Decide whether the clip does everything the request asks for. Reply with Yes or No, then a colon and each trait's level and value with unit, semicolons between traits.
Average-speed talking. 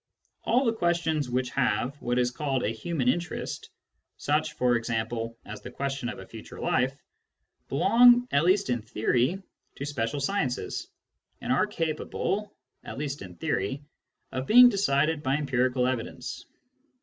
Yes: average, 155 wpm